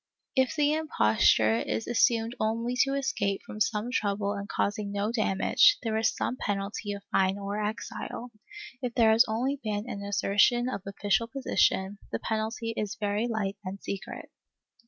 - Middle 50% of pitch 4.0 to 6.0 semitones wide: No, average, 3.0 semitones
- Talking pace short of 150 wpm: No, average, 160 wpm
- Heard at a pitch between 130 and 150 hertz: No, high, 215 Hz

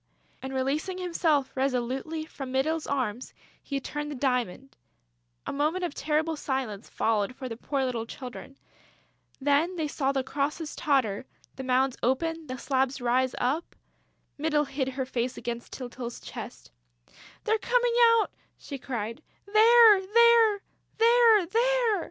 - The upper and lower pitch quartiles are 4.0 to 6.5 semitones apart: Yes, average, 4.8 semitones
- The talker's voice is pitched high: Yes, very high, 275 Hz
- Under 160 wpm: Yes, average, 140 wpm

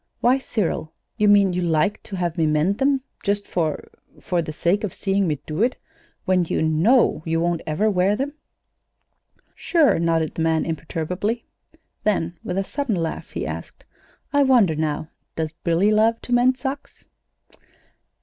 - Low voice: No, medium, 185 Hz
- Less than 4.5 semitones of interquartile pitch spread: No, average, 5.3 semitones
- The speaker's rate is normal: Yes, average, 165 wpm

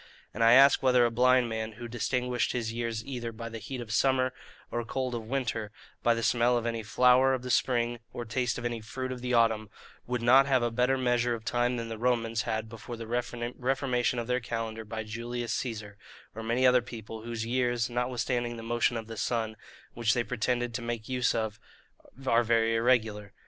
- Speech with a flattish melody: Yes, narrow, 1.6 semitones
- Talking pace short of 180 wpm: No, fast, 205 wpm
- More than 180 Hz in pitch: No, low, 120 Hz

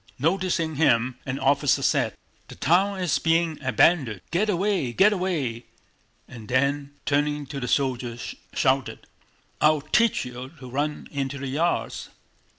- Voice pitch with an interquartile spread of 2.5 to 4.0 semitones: No, average, 4.4 semitones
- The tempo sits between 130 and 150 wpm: Yes, average, 140 wpm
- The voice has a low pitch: No, medium, 145 Hz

